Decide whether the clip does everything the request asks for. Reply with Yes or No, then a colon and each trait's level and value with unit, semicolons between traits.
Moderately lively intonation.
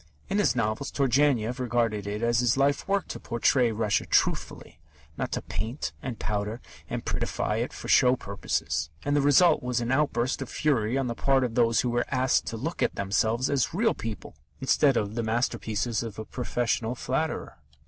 Yes: average, 3.4 semitones